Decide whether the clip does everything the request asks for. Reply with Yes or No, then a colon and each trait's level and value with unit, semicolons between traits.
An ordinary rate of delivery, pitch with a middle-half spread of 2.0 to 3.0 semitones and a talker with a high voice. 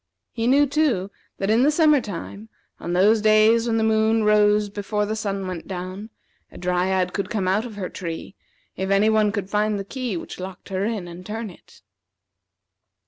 Yes: average, 195 wpm; average, 2.7 semitones; high, 210 Hz